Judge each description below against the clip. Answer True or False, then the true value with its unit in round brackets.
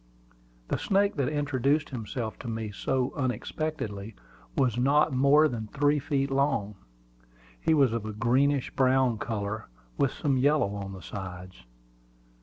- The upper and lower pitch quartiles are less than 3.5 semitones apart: False (4.7 semitones)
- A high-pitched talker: False (130 Hz)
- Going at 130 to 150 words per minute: True (140 wpm)